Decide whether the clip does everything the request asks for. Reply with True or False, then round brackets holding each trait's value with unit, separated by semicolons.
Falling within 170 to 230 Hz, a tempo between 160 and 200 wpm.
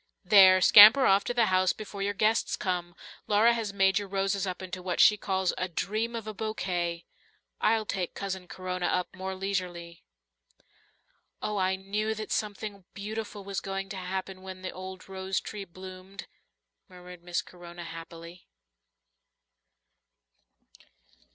False (190 Hz; 145 wpm)